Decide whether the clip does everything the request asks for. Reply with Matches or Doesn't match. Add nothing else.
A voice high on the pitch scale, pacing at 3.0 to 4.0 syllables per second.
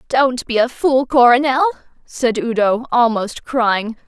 Matches